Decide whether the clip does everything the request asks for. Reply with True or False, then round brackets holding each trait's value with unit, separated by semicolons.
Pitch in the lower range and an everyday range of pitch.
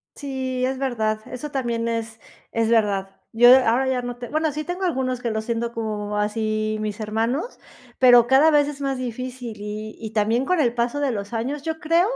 False (240 Hz; 3.5 semitones)